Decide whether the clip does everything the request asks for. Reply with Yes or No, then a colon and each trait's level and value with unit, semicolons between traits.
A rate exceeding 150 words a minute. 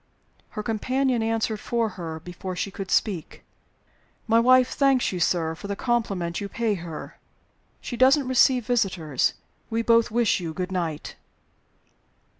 No: average, 145 wpm